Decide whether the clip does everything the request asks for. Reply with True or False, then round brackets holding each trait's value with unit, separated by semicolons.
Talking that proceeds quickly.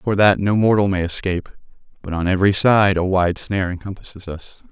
False (190 wpm)